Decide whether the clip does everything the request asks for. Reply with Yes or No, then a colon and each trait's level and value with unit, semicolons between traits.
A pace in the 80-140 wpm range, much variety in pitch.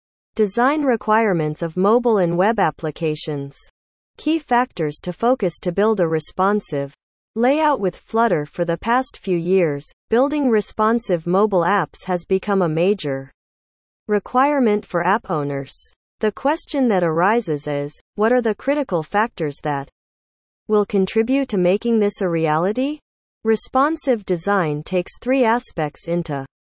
Yes: slow, 135 wpm; wide, 5.7 semitones